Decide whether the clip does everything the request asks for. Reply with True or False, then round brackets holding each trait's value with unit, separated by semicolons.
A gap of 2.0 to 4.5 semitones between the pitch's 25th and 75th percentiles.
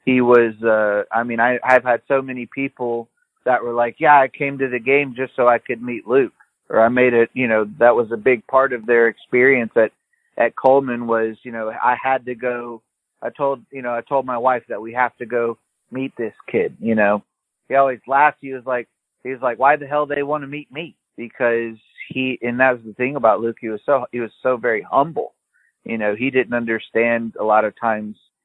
True (2.4 semitones)